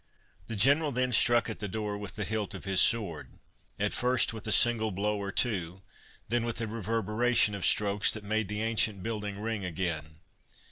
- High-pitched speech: No, low, 105 Hz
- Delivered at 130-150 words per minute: No, average, 185 wpm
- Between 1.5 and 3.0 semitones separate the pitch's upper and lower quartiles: Yes, narrow, 2.4 semitones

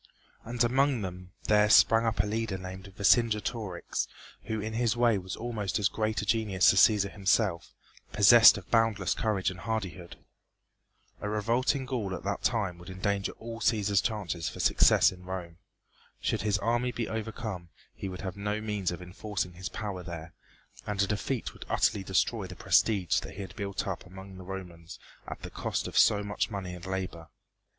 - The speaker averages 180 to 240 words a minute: Yes, average, 185 wpm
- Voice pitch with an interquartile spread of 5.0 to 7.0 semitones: No, average, 3.1 semitones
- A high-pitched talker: No, low, 100 Hz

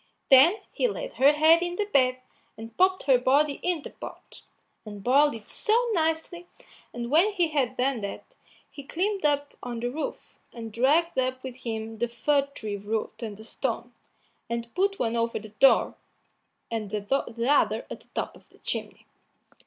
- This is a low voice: No, very high, 265 Hz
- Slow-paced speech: No, average, 180 wpm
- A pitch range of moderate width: No, wide, 5.8 semitones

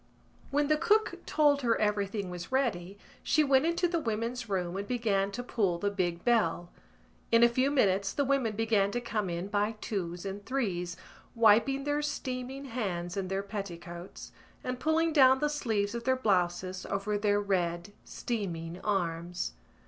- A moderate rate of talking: Yes, average, 165 wpm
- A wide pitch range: Yes, wide, 5.7 semitones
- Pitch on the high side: Yes, high, 210 Hz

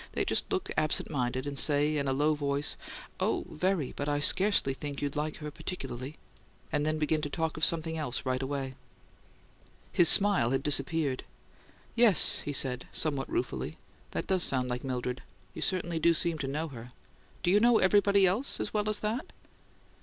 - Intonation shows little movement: No, average, 4.7 semitones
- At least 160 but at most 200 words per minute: Yes, average, 180 wpm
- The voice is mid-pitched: Yes, medium, 150 Hz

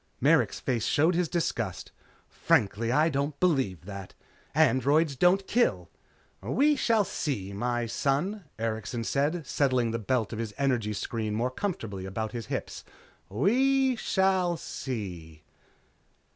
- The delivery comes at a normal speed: No, slow, 130 wpm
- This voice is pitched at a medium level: No, low, 130 Hz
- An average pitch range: No, wide, 7.8 semitones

